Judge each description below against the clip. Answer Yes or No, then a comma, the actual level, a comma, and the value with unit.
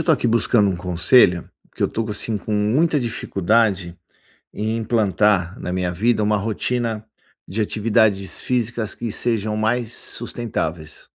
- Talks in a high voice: No, low, 110 Hz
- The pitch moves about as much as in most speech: Yes, average, 3.1 semitones